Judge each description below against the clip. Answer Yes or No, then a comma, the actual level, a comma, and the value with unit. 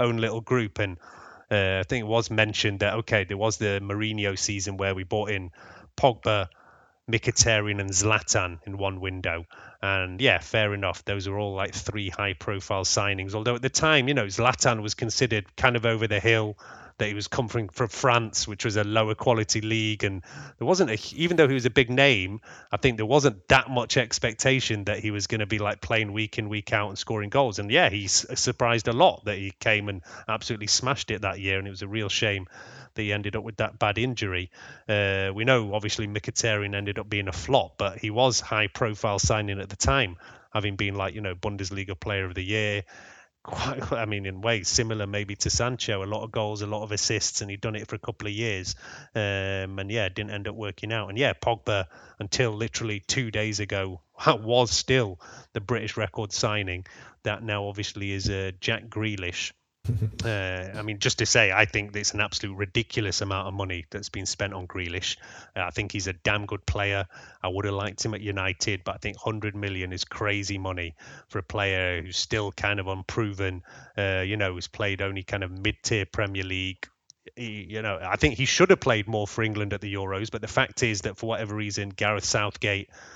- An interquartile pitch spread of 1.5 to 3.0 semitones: Yes, narrow, 2.4 semitones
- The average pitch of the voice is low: Yes, low, 105 Hz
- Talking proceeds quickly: Yes, fast, 215 wpm